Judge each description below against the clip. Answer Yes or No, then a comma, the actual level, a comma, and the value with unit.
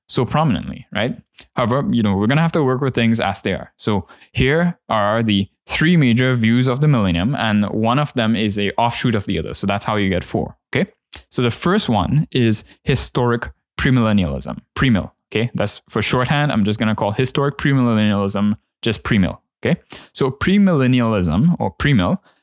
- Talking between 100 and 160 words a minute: No, average, 185 wpm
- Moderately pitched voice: No, low, 115 Hz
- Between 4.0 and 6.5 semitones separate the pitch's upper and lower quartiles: Yes, average, 4.3 semitones